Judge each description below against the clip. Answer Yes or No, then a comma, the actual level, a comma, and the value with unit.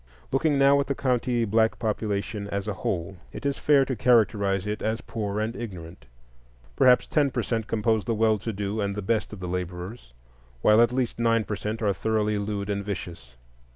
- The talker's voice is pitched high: No, low, 110 Hz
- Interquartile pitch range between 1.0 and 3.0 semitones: Yes, average, 2.7 semitones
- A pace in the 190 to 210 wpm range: Yes, average, 200 wpm